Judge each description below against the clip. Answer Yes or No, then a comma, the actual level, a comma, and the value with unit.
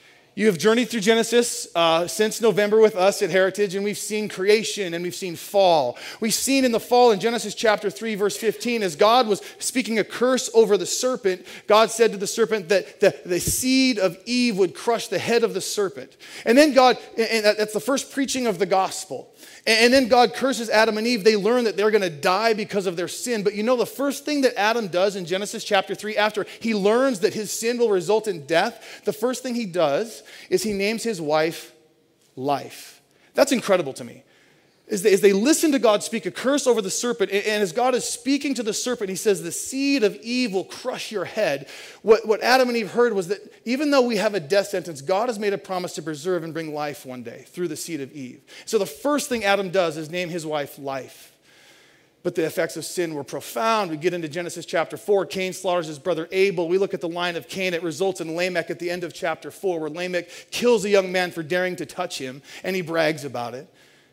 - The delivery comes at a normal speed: No, fast, 235 wpm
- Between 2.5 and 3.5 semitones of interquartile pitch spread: No, average, 4.5 semitones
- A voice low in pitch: No, high, 205 Hz